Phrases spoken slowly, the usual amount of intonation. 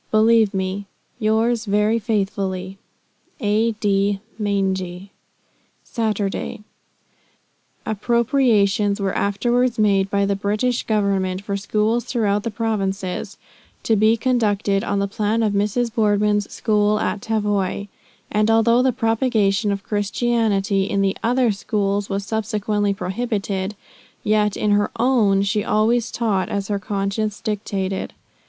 No: slow, 120 wpm; narrow, 2.0 semitones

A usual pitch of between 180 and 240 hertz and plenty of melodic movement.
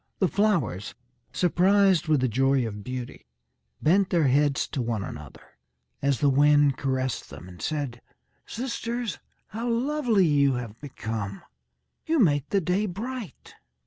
No: medium, 145 Hz; wide, 7.8 semitones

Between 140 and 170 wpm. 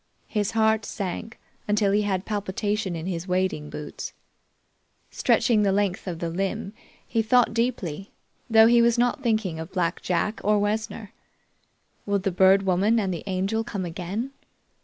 Yes: average, 160 wpm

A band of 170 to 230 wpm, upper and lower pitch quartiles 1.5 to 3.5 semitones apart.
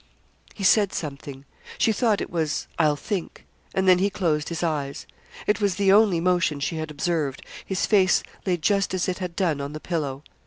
No: average, 195 wpm; average, 4.2 semitones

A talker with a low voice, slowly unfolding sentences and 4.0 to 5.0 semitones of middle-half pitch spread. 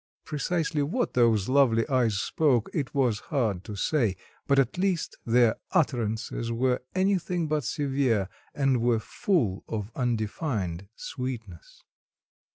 Yes: low, 125 Hz; slow, 125 wpm; average, 4.7 semitones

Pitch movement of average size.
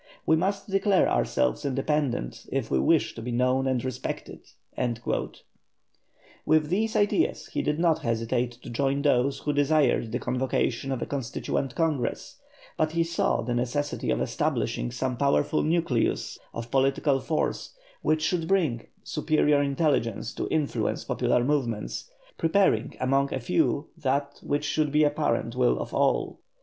Yes: average, 4.1 semitones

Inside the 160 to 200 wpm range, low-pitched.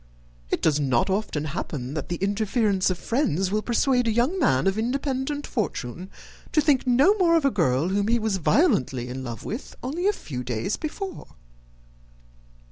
No: average, 175 wpm; high, 210 Hz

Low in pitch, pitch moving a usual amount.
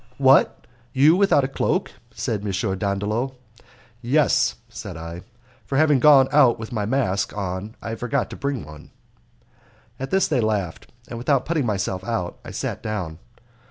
No: low, 115 Hz; wide, 5.7 semitones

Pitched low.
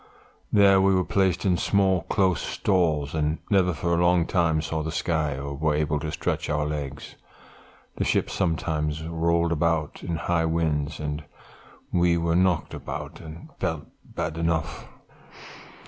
Yes: very low, 80 Hz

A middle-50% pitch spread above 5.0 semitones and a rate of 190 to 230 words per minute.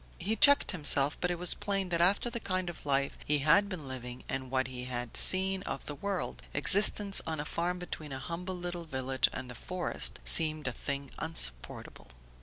Yes: wide, 5.6 semitones; average, 200 wpm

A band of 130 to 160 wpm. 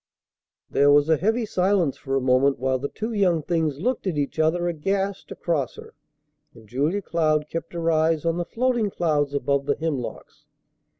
No: average, 180 wpm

